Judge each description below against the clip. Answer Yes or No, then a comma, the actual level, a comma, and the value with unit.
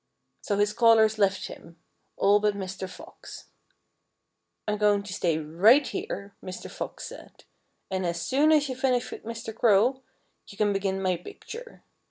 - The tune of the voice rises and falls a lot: No, average, 3.4 semitones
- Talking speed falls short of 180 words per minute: Yes, average, 160 wpm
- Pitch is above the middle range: Yes, high, 205 Hz